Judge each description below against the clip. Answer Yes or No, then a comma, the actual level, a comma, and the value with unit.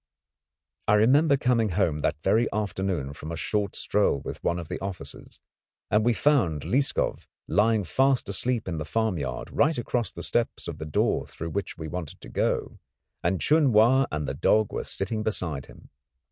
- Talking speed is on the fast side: No, average, 180 wpm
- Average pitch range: No, wide, 6.2 semitones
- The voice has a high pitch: No, low, 100 Hz